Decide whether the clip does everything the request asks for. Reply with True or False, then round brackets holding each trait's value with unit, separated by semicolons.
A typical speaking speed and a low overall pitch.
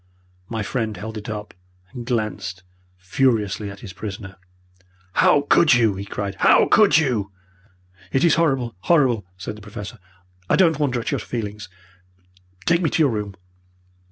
True (155 wpm; 110 Hz)